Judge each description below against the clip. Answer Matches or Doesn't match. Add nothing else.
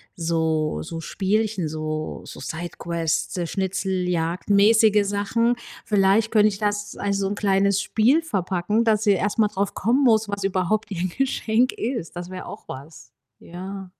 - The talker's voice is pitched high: Matches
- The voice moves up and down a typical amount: Matches